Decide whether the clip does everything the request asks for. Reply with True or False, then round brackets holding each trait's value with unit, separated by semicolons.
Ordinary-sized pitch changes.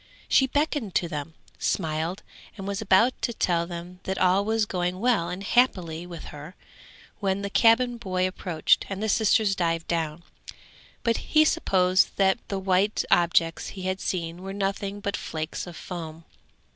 True (3.1 semitones)